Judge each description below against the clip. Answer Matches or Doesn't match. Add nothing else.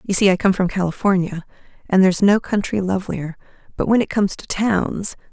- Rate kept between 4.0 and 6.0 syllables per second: Matches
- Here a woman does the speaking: Matches